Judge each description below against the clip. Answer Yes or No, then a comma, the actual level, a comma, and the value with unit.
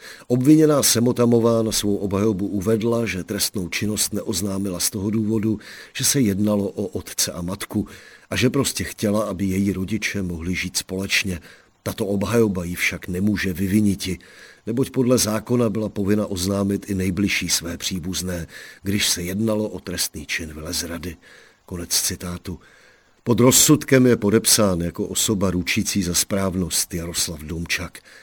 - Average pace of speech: Yes, average, 140 wpm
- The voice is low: Yes, low, 100 Hz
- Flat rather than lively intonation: No, average, 3.2 semitones